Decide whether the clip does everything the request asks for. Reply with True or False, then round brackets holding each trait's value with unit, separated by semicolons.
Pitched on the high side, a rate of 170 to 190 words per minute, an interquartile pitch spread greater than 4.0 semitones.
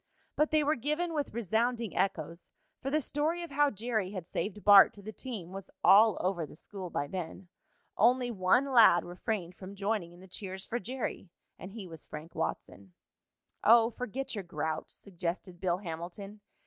True (200 Hz; 175 wpm; 5.3 semitones)